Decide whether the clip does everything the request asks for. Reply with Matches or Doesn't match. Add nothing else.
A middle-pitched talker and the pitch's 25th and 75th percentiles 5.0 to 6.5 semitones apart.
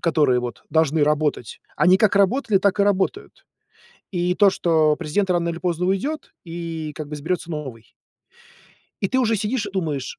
Doesn't match